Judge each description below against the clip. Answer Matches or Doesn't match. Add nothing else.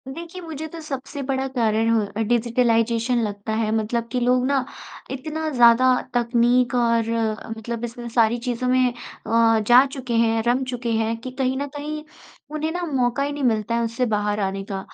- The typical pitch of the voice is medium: Doesn't match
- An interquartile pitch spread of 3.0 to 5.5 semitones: Doesn't match